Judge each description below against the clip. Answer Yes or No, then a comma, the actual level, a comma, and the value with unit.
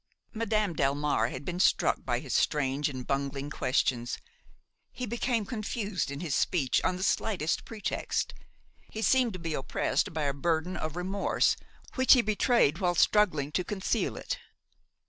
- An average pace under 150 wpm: No, average, 155 wpm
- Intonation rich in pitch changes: Yes, wide, 6.9 semitones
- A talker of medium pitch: Yes, medium, 175 Hz